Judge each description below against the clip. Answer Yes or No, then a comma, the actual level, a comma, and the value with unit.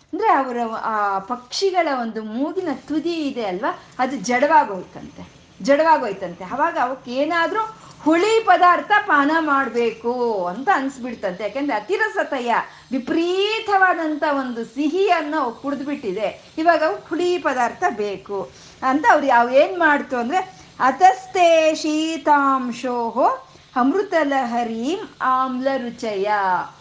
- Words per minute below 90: No, average, 95 wpm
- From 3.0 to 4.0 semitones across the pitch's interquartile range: No, wide, 5.5 semitones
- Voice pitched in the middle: No, very high, 280 Hz